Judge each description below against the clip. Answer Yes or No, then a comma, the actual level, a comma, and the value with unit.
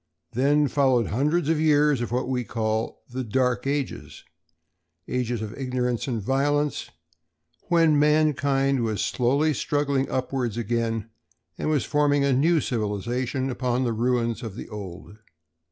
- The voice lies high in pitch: No, low, 125 Hz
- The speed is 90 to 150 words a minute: Yes, slow, 135 wpm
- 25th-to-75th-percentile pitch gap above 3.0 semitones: Yes, average, 3.8 semitones